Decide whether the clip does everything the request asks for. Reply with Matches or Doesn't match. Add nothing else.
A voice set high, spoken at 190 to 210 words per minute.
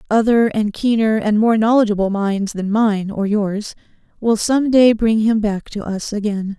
Doesn't match